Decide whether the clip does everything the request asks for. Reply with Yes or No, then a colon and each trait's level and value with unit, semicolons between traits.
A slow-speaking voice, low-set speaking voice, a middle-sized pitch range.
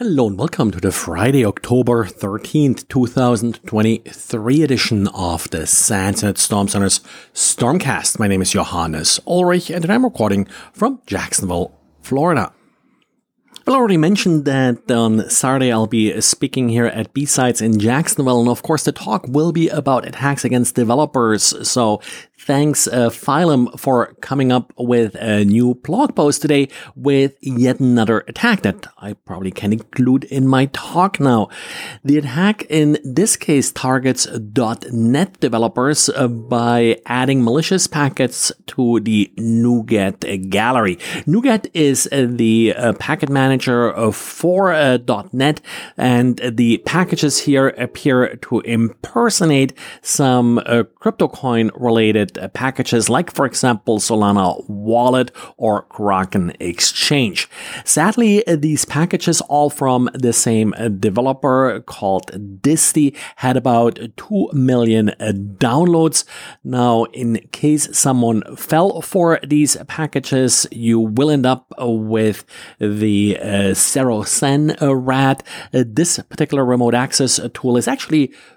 Yes: slow, 120 wpm; low, 125 Hz; average, 4.4 semitones